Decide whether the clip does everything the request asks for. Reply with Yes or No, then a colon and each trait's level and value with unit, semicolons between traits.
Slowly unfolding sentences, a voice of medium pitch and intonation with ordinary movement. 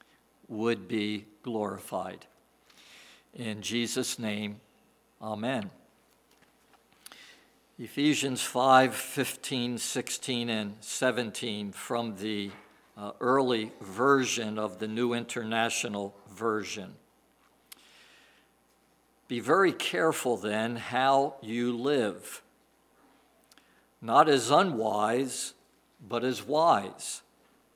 No: slow, 80 wpm; low, 115 Hz; average, 3.0 semitones